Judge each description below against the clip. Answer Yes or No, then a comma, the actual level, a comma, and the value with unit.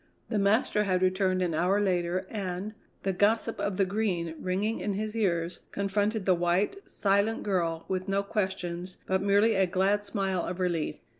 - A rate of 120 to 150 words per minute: No, average, 170 wpm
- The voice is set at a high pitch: Yes, high, 195 Hz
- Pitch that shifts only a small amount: Yes, narrow, 2.1 semitones